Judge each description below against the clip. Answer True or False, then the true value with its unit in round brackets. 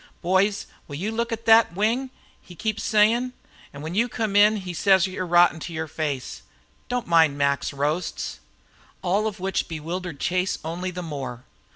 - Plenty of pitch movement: False (4.8 semitones)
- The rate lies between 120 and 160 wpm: False (175 wpm)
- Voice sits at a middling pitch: True (180 Hz)